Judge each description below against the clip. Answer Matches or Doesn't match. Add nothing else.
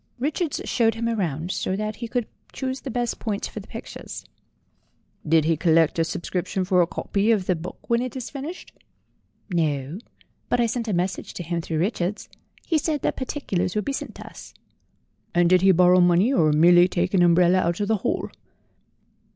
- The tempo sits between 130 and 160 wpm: Doesn't match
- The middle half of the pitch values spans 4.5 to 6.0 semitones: Matches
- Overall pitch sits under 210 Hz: Matches